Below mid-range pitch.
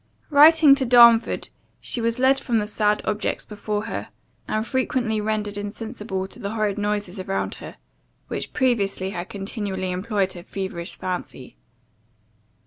No: high, 210 Hz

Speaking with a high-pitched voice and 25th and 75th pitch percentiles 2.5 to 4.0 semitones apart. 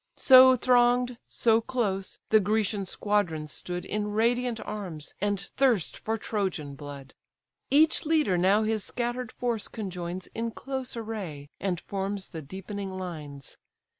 No: high, 205 Hz; average, 4.6 semitones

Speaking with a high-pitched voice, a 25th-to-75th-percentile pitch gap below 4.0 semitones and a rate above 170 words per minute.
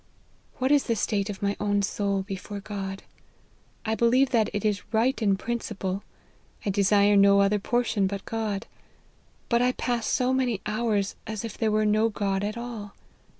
Yes: high, 210 Hz; narrow, 2.6 semitones; average, 180 wpm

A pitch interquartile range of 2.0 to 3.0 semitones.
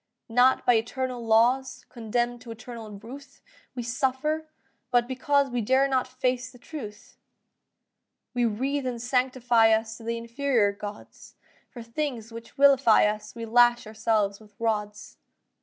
Yes: narrow, 2.6 semitones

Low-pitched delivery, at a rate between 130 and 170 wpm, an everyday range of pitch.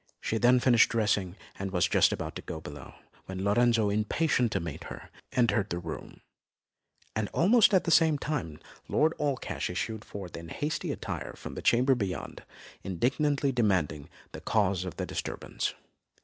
No: low, 110 Hz; average, 165 wpm; wide, 6.2 semitones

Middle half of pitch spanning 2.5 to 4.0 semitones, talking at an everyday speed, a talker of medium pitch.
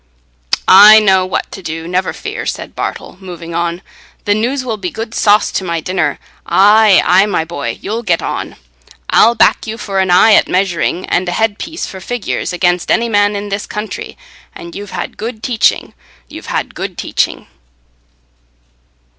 No: average, 3.5 semitones; average, 170 wpm; high, 195 Hz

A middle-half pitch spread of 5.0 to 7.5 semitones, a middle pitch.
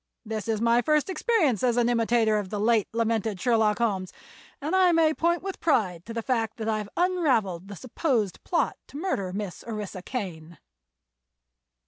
No: wide, 5.4 semitones; high, 230 Hz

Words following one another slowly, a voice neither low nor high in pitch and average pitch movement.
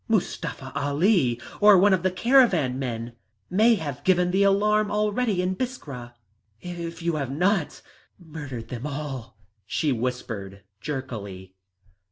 No: slow, 130 wpm; medium, 160 Hz; wide, 7.7 semitones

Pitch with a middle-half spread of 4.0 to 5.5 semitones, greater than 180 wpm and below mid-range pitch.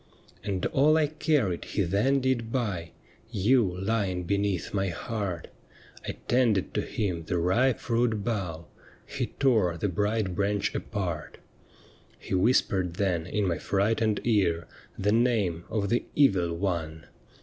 No: average, 4.3 semitones; average, 150 wpm; low, 100 Hz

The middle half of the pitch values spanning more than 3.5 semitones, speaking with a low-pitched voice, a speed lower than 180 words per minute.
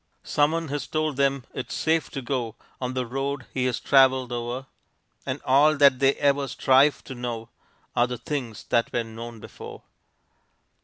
No: narrow, 2.6 semitones; low, 130 Hz; average, 165 wpm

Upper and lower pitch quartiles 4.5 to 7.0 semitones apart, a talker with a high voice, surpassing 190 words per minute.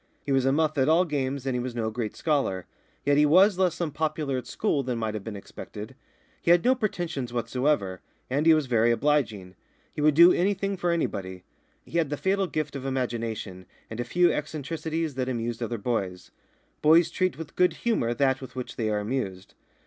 No: wide, 5.6 semitones; low, 135 Hz; average, 200 wpm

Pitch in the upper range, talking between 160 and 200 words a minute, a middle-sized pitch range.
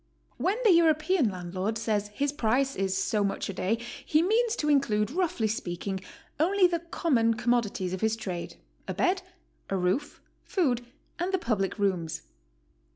No: high, 230 Hz; average, 165 wpm; wide, 8.8 semitones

